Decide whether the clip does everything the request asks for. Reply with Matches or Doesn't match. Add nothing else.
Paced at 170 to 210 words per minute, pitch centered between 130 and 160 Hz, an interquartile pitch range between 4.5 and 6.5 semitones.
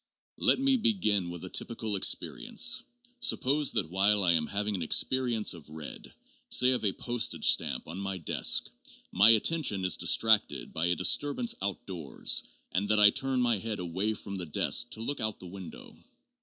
Doesn't match